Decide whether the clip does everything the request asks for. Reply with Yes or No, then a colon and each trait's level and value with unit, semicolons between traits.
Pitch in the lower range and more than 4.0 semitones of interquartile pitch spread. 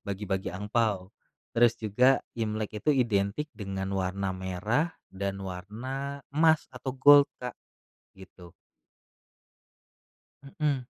Yes: low, 105 Hz; wide, 5.5 semitones